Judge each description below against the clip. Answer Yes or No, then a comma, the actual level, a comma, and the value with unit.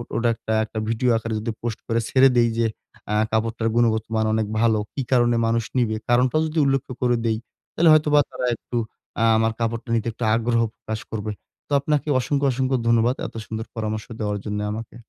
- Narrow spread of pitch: Yes, narrow, 2.2 semitones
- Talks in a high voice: No, low, 115 Hz